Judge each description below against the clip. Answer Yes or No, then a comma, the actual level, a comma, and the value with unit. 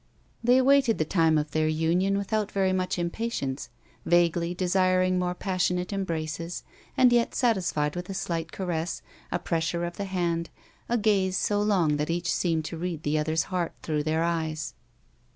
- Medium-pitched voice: Yes, medium, 175 Hz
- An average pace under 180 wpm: Yes, average, 170 wpm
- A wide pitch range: No, average, 3.0 semitones